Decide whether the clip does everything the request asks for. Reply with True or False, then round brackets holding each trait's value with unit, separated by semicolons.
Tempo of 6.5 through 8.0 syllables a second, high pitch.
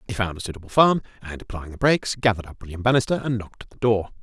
False (7.5 syllables/s; 105 Hz)